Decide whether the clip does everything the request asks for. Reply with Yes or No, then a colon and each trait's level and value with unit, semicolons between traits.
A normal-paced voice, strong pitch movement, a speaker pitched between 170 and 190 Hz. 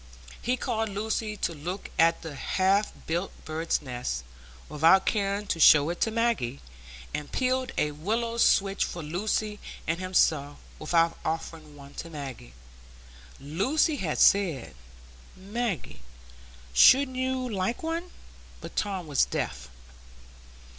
No: slow, 125 wpm; wide, 6.5 semitones; medium, 185 Hz